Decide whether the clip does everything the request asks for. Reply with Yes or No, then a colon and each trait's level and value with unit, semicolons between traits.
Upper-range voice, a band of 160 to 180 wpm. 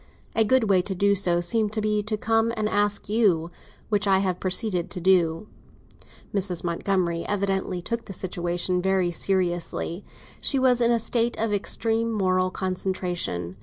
Yes: high, 195 Hz; average, 165 wpm